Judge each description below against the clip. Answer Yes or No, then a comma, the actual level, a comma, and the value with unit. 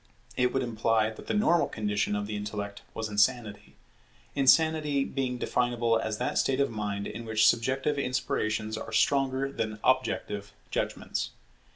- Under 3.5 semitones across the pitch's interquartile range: No, average, 3.8 semitones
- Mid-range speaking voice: No, low, 115 Hz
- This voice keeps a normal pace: Yes, average, 150 wpm